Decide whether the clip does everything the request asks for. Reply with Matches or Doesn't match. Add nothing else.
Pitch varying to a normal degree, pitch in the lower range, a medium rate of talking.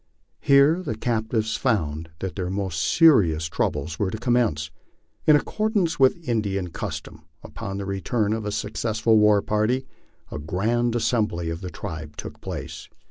Matches